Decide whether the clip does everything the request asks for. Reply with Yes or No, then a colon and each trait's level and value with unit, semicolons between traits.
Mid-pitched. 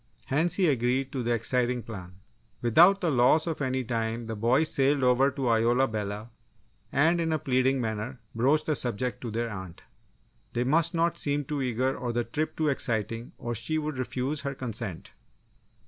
No: low, 130 Hz